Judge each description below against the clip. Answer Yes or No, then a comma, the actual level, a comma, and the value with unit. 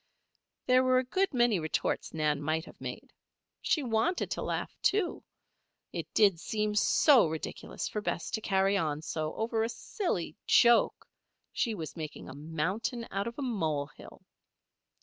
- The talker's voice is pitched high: Yes, high, 210 Hz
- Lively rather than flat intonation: Yes, wide, 7.1 semitones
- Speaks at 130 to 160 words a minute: Yes, average, 155 wpm